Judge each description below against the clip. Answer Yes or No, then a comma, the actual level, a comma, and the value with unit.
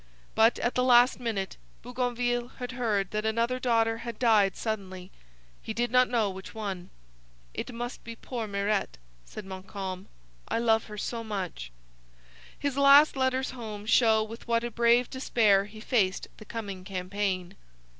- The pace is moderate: Yes, average, 155 wpm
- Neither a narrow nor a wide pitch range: Yes, average, 3.3 semitones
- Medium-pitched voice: No, high, 225 Hz